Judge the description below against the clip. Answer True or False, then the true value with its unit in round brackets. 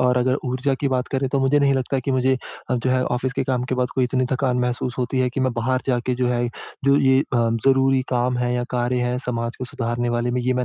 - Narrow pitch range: True (1.2 semitones)